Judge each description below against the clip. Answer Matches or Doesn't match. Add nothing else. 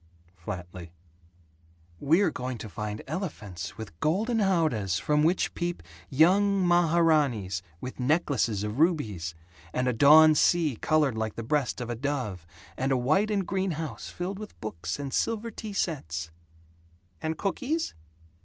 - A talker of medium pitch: Matches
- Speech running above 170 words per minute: Doesn't match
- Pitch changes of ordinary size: Doesn't match